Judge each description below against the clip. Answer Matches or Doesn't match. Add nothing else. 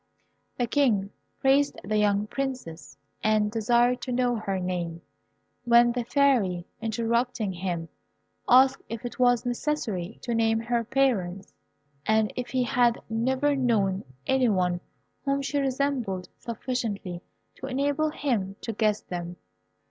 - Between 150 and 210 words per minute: Doesn't match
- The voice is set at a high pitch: Matches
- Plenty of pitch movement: Doesn't match